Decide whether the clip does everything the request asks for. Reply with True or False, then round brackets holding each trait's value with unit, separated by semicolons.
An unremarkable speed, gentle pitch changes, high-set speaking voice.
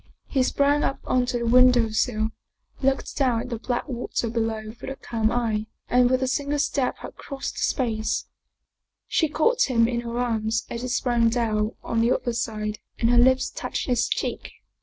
True (190 wpm; 2.3 semitones; 240 Hz)